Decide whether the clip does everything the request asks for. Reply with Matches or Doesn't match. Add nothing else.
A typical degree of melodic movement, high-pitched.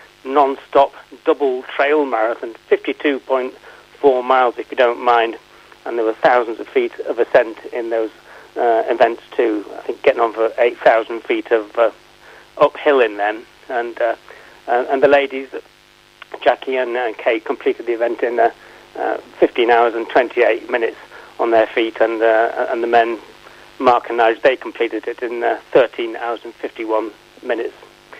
Doesn't match